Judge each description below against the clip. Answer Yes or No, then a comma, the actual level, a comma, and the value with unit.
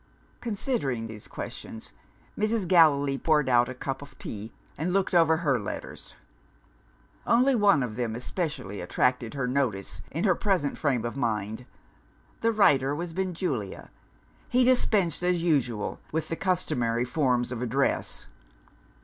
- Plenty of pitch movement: Yes, wide, 6.7 semitones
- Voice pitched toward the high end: No, medium, 140 Hz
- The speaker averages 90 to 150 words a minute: Yes, average, 140 wpm